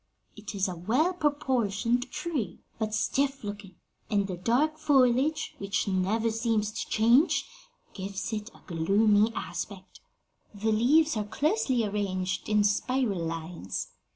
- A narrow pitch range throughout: No, average, 4.5 semitones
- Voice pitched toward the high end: Yes, high, 215 Hz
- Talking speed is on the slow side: Yes, slow, 130 wpm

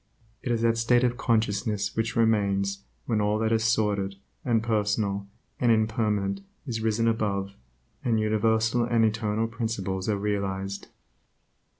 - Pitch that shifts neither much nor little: No, narrow, 2.1 semitones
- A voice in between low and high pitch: No, low, 110 Hz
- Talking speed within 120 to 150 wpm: Yes, slow, 135 wpm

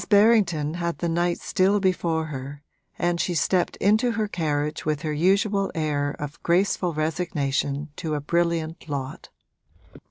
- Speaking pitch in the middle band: Yes, medium, 165 Hz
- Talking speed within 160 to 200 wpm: No, average, 140 wpm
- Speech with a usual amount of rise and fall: Yes, average, 3.7 semitones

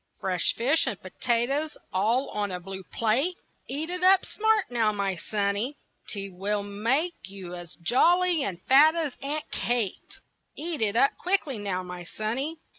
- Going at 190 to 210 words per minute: No, average, 160 wpm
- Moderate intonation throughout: No, wide, 7.4 semitones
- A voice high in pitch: Yes, high, 230 Hz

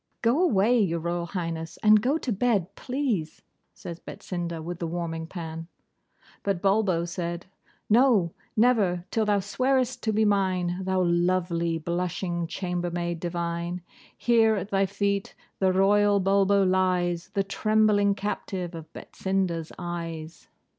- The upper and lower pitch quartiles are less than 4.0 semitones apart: Yes, average, 3.0 semitones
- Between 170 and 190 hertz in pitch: Yes, medium, 185 Hz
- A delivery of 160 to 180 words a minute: No, slow, 135 wpm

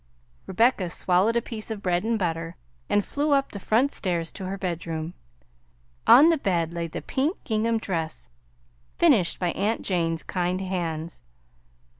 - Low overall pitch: No, medium, 185 Hz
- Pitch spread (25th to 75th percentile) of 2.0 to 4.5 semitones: No, average, 4.9 semitones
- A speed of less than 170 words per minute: Yes, average, 155 wpm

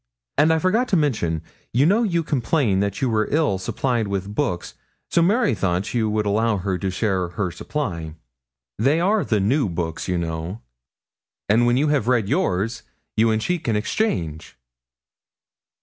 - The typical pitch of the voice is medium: No, low, 110 Hz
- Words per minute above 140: Yes, average, 170 wpm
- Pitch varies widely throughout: Yes, wide, 7.6 semitones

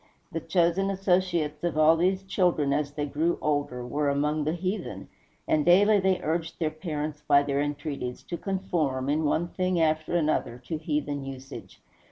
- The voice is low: No, medium, 155 Hz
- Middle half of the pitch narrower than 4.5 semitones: Yes, average, 3.2 semitones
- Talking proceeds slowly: No, average, 170 wpm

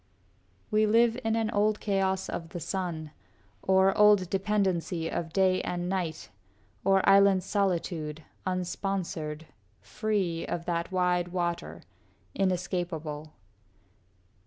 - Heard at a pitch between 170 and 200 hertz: Yes, medium, 185 Hz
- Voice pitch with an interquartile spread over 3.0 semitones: No, narrow, 2.6 semitones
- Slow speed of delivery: Yes, slow, 110 wpm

